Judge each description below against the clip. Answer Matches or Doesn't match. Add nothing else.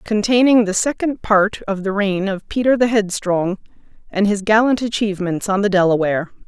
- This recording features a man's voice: Doesn't match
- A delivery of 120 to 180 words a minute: Matches